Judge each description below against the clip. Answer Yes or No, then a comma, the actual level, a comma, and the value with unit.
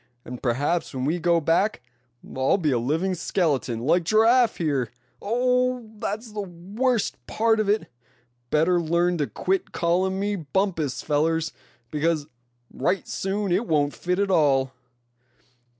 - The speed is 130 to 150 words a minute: Yes, slow, 135 wpm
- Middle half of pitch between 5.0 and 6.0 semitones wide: Yes, average, 5.3 semitones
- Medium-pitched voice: Yes, medium, 175 Hz